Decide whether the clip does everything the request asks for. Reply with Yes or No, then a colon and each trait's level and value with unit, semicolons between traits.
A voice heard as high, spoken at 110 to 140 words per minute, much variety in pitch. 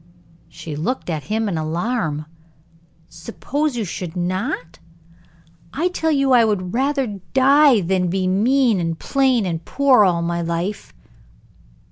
Yes: high, 200 Hz; slow, 135 wpm; wide, 7.4 semitones